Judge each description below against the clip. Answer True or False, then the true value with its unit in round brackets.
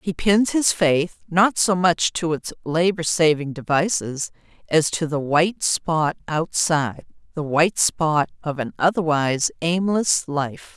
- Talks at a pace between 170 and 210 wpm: False (145 wpm)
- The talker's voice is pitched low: False (165 Hz)